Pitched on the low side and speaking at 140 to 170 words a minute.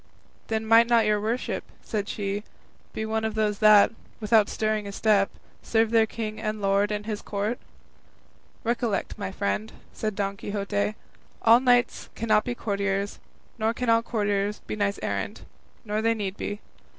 No: high, 215 Hz; average, 165 wpm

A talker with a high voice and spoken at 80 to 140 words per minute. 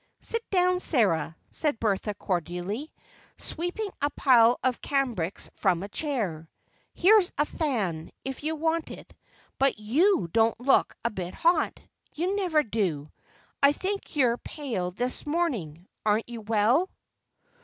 Yes: high, 245 Hz; slow, 135 wpm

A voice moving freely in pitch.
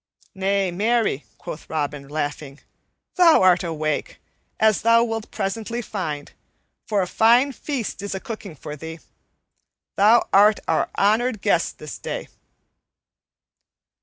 Yes: wide, 5.9 semitones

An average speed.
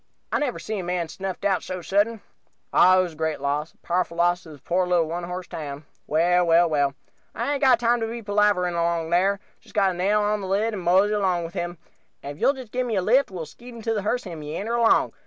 No: fast, 255 wpm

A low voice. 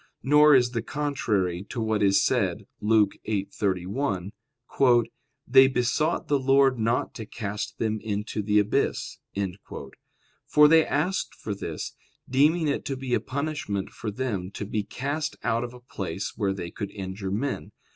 Yes: low, 115 Hz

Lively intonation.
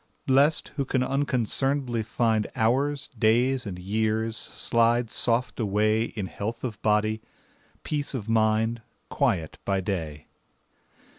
No: average, 2.9 semitones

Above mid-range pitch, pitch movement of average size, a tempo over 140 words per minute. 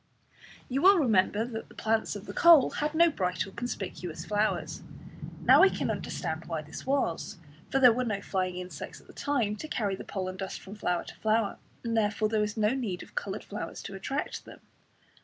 Yes: high, 210 Hz; average, 4.7 semitones; fast, 205 wpm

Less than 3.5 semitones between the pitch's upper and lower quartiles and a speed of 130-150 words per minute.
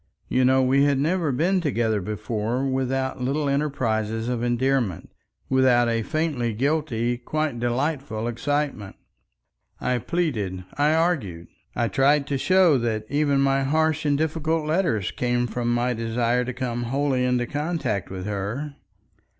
No: average, 3.8 semitones; average, 140 wpm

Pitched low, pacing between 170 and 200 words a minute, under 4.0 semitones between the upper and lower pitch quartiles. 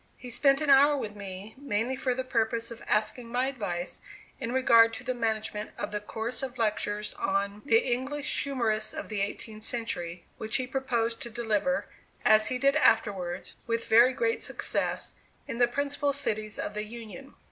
No: high, 230 Hz; average, 180 wpm; average, 3.5 semitones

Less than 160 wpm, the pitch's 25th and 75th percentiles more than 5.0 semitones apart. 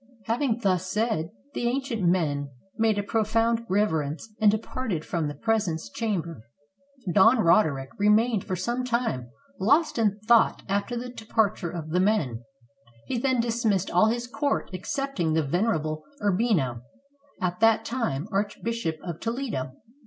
Yes: average, 140 wpm; wide, 5.5 semitones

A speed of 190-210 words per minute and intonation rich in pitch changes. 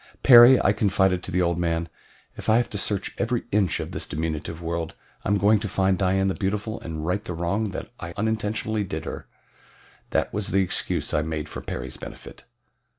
No: average, 200 wpm; average, 3.8 semitones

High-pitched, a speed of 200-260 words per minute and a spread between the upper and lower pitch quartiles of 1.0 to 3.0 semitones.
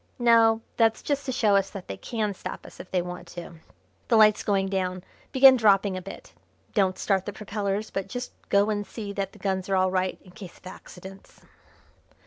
Yes: high, 200 Hz; fast, 205 wpm; narrow, 2.6 semitones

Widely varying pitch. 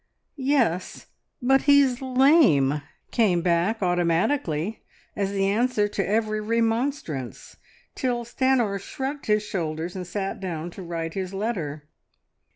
Yes: wide, 5.8 semitones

